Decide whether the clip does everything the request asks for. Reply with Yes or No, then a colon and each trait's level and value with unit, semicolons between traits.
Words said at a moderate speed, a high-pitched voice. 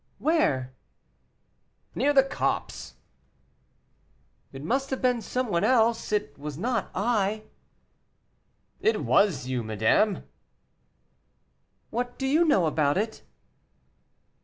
No: slow, 105 wpm; high, 215 Hz